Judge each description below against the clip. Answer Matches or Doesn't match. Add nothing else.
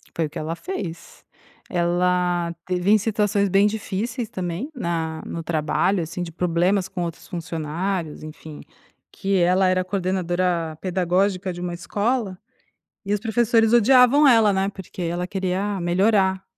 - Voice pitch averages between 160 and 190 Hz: Matches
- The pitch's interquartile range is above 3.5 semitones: Doesn't match